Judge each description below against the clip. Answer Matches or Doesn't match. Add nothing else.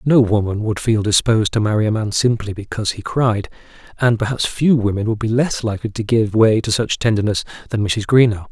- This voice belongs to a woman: Doesn't match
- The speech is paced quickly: Matches